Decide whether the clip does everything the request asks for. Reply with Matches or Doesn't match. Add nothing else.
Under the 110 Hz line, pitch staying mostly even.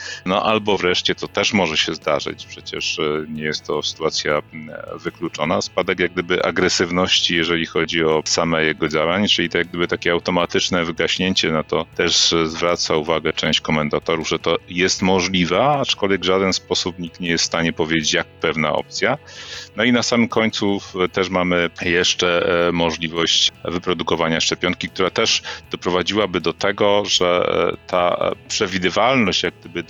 Matches